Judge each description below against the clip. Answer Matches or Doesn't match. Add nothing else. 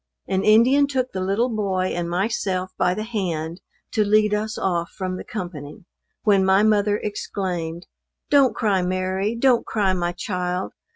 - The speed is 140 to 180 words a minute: Matches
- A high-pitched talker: Matches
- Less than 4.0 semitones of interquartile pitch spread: Matches